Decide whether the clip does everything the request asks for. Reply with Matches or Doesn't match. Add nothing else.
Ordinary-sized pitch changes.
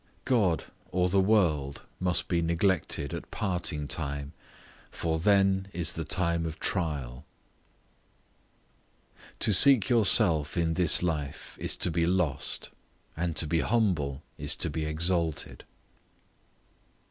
Matches